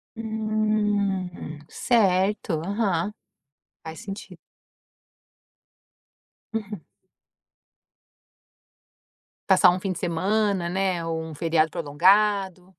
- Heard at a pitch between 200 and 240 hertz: No, high, 190 Hz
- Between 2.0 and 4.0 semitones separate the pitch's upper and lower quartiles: Yes, average, 3.5 semitones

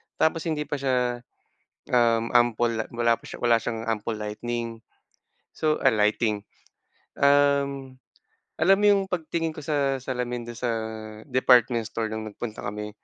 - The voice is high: No, low, 120 Hz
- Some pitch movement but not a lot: Yes, average, 3.6 semitones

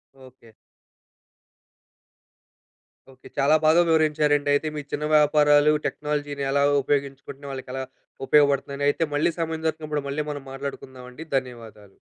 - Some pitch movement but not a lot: No, narrow, 2.0 semitones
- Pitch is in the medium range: Yes, medium, 145 Hz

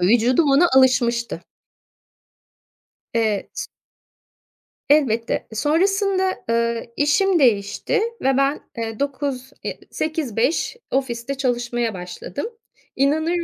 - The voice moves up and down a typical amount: Yes, average, 4.4 semitones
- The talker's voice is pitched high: Yes, very high, 260 Hz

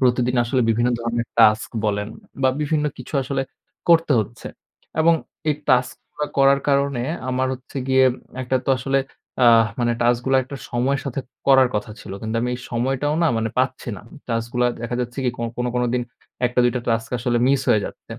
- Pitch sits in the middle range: No, low, 125 Hz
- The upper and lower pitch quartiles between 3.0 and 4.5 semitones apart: No, narrow, 2.4 semitones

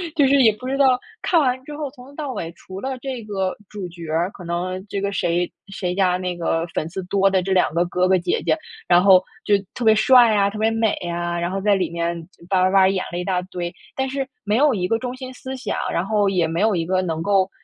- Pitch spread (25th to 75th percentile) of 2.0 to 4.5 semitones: No, average, 5.1 semitones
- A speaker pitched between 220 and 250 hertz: No, high, 195 Hz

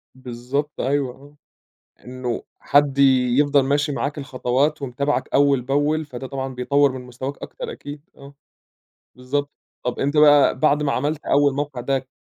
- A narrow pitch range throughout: Yes, narrow, 1.9 semitones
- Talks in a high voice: No, medium, 140 Hz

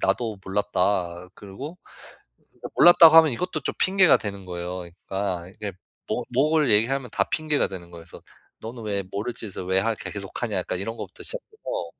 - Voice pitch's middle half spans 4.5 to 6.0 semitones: No, wide, 6.8 semitones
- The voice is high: No, low, 105 Hz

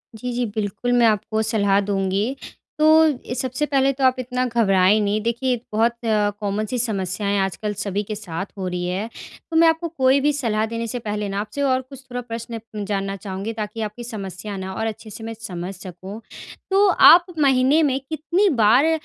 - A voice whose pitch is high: Yes, high, 220 Hz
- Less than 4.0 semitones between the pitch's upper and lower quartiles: No, average, 4.3 semitones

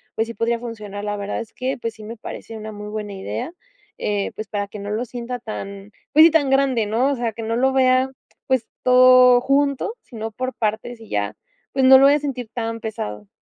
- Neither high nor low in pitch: No, high, 230 Hz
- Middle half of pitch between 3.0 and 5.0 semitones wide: Yes, average, 3.3 semitones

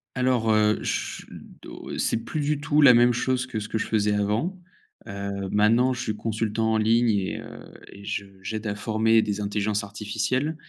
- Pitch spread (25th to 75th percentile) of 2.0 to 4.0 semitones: Yes, average, 2.9 semitones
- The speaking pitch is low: Yes, low, 110 Hz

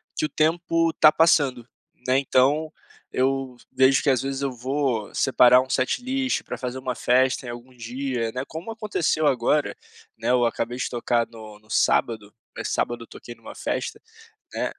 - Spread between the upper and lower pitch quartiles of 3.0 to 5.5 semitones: Yes, average, 3.4 semitones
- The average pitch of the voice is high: No, low, 130 Hz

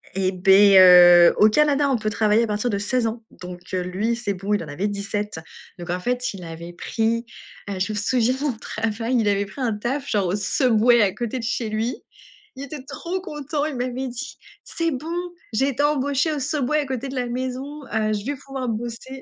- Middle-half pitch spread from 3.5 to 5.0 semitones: Yes, average, 4.6 semitones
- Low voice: No, high, 230 Hz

